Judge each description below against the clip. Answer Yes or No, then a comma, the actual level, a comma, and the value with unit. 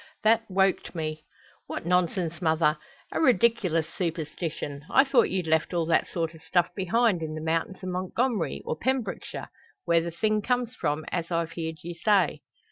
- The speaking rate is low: No, average, 170 wpm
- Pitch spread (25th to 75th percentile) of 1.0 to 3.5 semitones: No, average, 3.9 semitones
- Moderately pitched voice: Yes, medium, 170 Hz